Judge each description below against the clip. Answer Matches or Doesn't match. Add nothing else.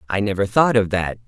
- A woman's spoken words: Doesn't match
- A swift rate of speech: Matches